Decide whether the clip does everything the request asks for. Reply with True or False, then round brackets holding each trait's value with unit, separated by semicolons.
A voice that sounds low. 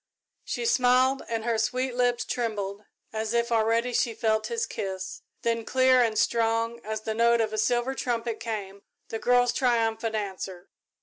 False (230 Hz)